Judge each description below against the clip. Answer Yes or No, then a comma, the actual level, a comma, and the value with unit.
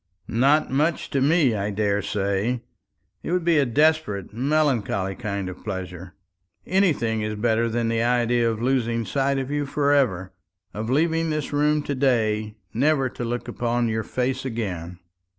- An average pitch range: Yes, average, 4.9 semitones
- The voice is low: Yes, low, 120 Hz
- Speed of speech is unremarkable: Yes, average, 160 wpm